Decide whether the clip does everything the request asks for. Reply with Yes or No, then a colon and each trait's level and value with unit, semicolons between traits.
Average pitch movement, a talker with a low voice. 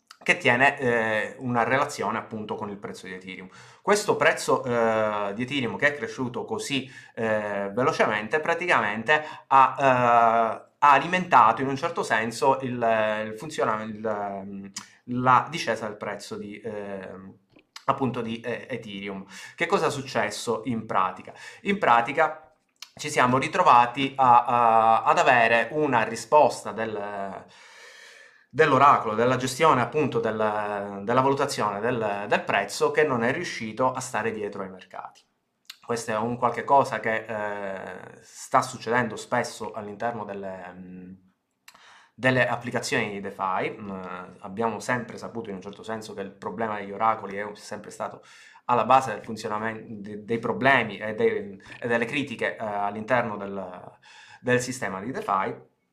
Yes: average, 4.0 semitones; low, 115 Hz